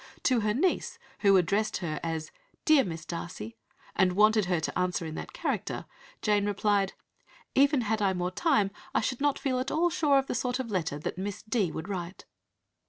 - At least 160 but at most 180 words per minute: No, average, 195 wpm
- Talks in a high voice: Yes, high, 205 Hz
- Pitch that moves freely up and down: Yes, wide, 5.9 semitones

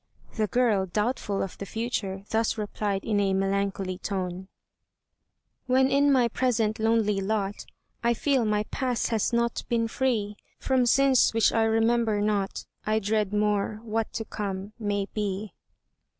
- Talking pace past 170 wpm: No, average, 150 wpm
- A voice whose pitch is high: Yes, high, 215 Hz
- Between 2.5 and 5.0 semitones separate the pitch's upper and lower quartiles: Yes, average, 2.8 semitones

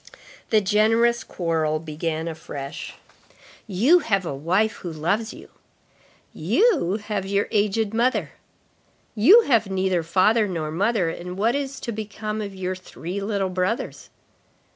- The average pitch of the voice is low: No, high, 200 Hz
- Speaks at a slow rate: Yes, slow, 130 wpm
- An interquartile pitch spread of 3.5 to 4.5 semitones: Yes, average, 4.2 semitones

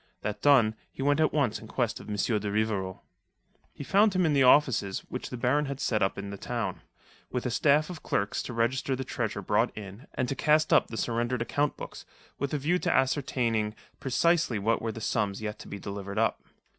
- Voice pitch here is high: No, low, 125 Hz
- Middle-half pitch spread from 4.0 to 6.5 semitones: Yes, average, 5.1 semitones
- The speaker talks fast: Yes, fast, 220 wpm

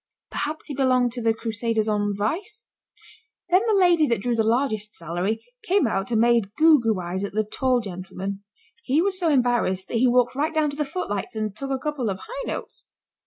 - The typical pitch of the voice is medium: No, high, 240 Hz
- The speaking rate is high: Yes, fast, 210 wpm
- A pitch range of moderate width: No, wide, 5.8 semitones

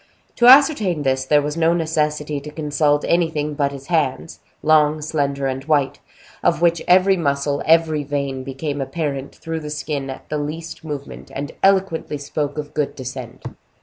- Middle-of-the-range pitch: Yes, medium, 150 Hz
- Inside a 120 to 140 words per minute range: No, average, 165 wpm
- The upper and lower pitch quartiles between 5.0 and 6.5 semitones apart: No, narrow, 2.4 semitones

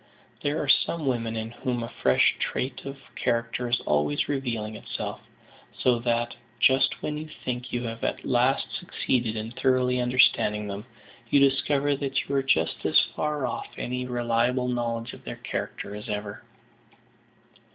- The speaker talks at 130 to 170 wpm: Yes, average, 160 wpm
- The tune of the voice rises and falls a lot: No, narrow, 2.6 semitones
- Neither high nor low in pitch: No, low, 125 Hz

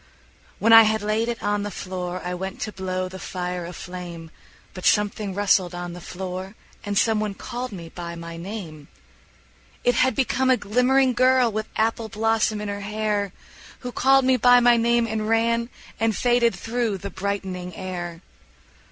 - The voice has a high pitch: Yes, high, 210 Hz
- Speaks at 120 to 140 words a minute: No, average, 175 wpm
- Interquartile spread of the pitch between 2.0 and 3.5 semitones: No, average, 4.1 semitones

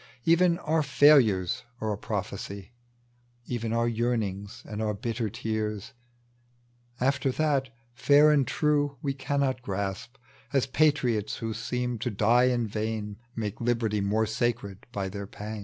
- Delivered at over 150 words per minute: No, average, 140 wpm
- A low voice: Yes, low, 115 Hz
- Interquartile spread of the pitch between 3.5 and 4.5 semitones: Yes, average, 4.2 semitones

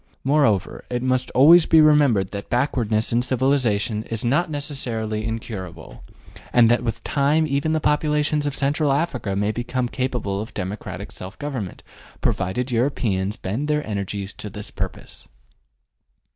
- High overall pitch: No, low, 125 Hz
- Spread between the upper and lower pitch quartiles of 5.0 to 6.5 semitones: Yes, average, 5.3 semitones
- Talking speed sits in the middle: Yes, average, 145 wpm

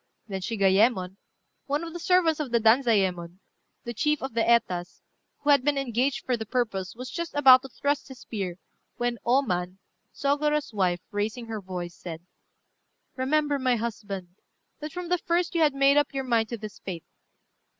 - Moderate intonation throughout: No, wide, 6.2 semitones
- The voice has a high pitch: Yes, high, 240 Hz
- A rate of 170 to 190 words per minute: Yes, average, 175 wpm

